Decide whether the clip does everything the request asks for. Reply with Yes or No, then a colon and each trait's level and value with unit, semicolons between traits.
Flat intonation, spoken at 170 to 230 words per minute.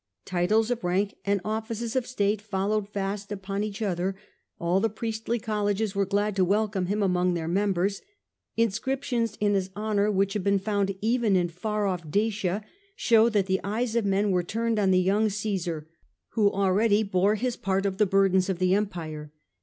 Yes: narrow, 2.3 semitones; average, 200 wpm